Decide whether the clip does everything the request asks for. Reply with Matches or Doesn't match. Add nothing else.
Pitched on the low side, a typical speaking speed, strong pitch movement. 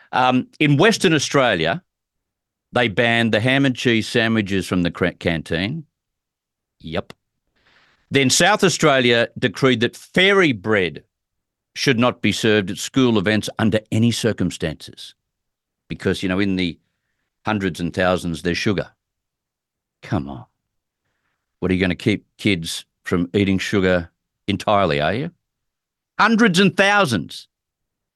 Doesn't match